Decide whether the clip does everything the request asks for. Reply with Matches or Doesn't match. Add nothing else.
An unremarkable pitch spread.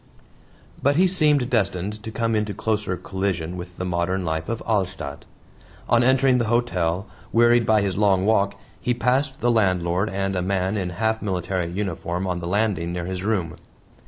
Matches